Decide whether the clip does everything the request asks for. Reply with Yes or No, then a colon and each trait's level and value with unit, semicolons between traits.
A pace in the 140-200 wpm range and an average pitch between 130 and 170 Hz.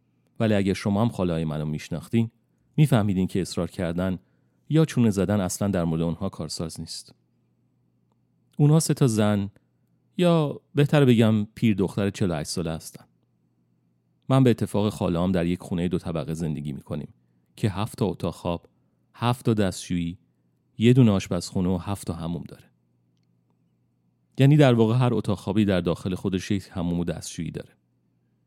No: fast, 155 wpm; very low, 95 Hz